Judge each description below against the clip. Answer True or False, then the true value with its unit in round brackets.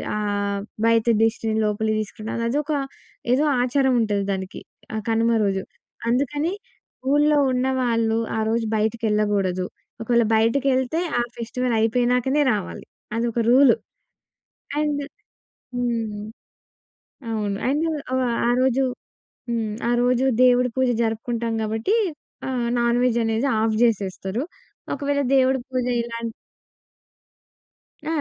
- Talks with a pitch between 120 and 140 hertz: False (235 Hz)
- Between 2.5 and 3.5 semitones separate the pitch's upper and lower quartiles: True (2.8 semitones)